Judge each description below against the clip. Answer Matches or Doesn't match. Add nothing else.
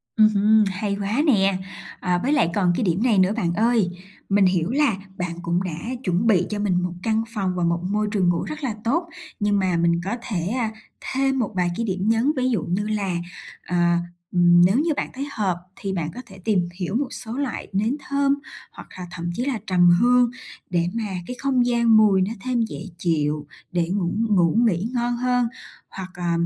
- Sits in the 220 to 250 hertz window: Doesn't match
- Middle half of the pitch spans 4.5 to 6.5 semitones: Matches